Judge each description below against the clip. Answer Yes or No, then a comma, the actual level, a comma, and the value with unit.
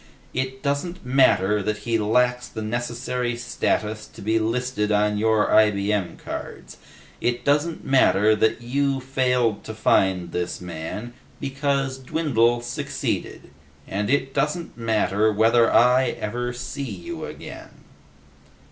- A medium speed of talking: No, slow, 125 wpm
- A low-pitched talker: Yes, low, 120 Hz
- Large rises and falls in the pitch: No, average, 3.7 semitones